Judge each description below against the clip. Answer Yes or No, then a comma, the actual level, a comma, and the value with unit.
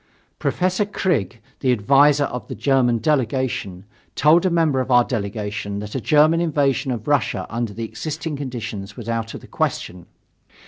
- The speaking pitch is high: No, low, 130 Hz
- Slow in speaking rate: No, average, 165 wpm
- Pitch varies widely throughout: No, average, 5.0 semitones